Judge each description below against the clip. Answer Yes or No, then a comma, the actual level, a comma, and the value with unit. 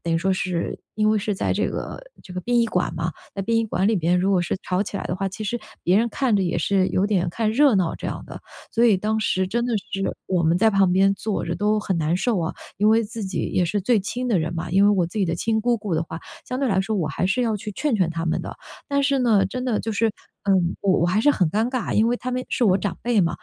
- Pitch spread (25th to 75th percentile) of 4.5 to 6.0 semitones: No, average, 3.8 semitones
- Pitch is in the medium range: No, high, 200 Hz